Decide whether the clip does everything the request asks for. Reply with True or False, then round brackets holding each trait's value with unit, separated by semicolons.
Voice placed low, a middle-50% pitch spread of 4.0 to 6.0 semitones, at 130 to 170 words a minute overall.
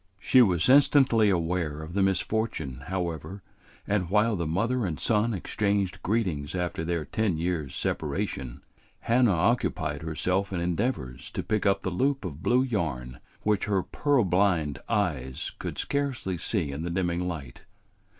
True (90 Hz; 5.0 semitones; 150 wpm)